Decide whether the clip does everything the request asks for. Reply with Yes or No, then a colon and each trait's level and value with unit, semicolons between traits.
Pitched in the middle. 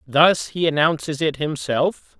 Yes: medium, 155 Hz